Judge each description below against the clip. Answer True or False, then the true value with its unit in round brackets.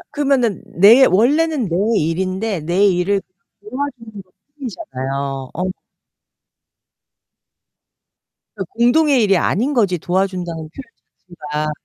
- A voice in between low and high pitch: False (195 Hz)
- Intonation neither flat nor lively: False (5.8 semitones)